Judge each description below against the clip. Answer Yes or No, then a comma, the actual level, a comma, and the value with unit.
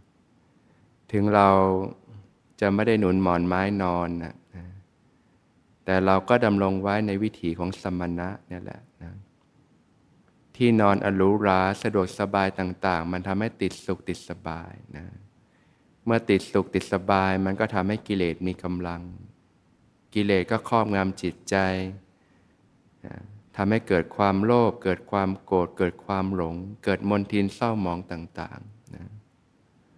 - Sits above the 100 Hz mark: No, very low, 95 Hz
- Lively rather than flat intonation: No, narrow, 2.4 semitones